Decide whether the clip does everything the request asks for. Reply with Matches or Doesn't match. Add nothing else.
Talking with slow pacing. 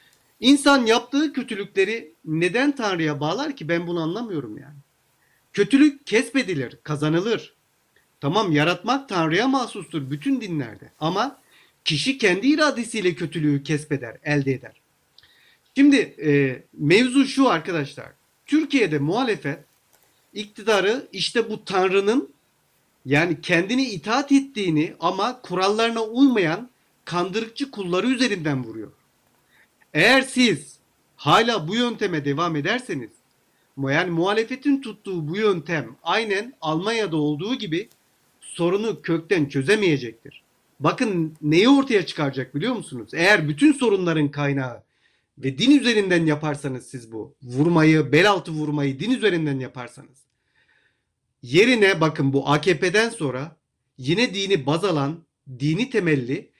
Doesn't match